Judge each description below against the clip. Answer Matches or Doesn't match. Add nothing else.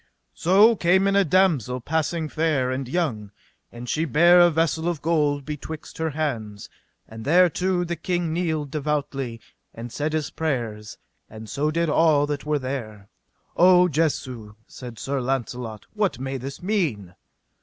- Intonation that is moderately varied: Matches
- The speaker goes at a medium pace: Matches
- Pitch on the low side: Doesn't match